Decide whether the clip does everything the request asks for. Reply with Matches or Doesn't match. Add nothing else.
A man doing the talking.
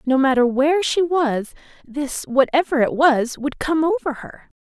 Doesn't match